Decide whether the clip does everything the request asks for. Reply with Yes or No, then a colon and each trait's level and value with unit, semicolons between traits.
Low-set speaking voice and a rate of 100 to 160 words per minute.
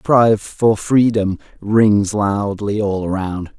Yes: low, 105 Hz; slow, 135 wpm